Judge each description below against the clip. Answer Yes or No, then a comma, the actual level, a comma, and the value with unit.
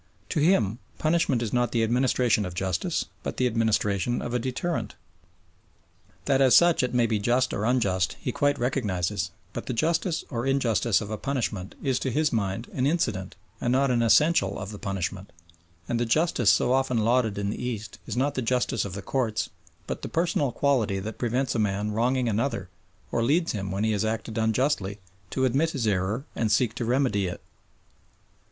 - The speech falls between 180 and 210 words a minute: Yes, average, 190 wpm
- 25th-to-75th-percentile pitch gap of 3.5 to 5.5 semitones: Yes, average, 4.1 semitones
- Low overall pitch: Yes, low, 120 Hz